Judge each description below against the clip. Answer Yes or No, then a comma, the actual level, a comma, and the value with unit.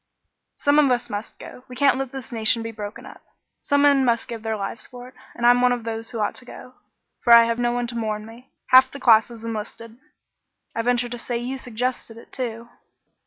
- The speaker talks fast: Yes, fast, 235 wpm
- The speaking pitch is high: Yes, high, 240 Hz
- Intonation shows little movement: Yes, narrow, 1.8 semitones